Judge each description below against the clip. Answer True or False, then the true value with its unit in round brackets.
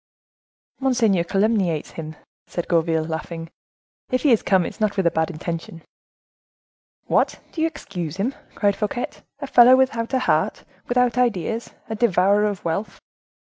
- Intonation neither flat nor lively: False (5.9 semitones)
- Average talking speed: True (155 wpm)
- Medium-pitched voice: False (200 Hz)